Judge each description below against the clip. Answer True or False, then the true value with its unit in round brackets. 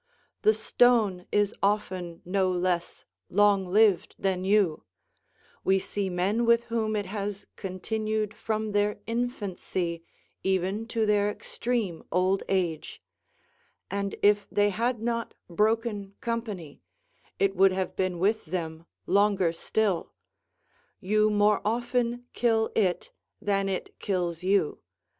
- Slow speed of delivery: True (120 wpm)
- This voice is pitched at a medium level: False (200 Hz)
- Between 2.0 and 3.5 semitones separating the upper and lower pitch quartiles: True (2.8 semitones)